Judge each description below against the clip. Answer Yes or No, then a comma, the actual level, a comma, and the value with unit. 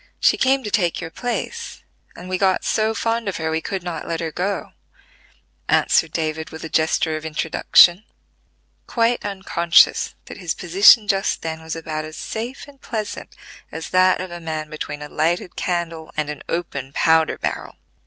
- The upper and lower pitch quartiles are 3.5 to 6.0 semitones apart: Yes, average, 3.9 semitones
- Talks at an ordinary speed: Yes, average, 175 wpm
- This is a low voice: No, medium, 170 Hz